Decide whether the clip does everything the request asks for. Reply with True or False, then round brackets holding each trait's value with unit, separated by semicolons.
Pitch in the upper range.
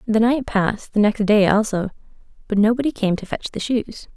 True (215 Hz)